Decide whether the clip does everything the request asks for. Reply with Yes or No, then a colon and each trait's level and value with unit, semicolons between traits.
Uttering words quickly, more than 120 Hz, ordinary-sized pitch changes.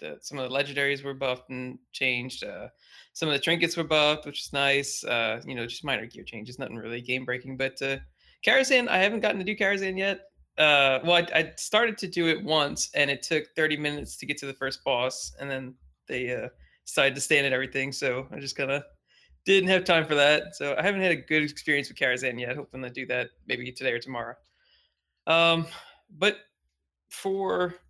Yes: fast, 215 wpm; medium, 140 Hz; average, 4.6 semitones